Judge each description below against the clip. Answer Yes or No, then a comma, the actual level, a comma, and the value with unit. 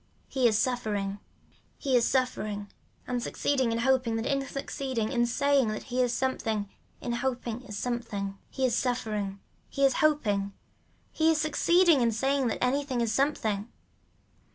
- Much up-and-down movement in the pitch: No, average, 3.6 semitones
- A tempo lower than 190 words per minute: Yes, average, 155 wpm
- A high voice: Yes, high, 245 Hz